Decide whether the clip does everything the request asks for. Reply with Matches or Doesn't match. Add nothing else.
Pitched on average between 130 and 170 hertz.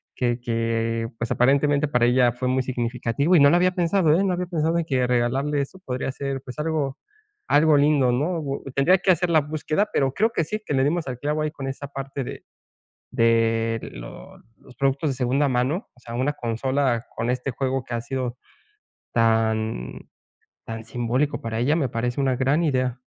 Matches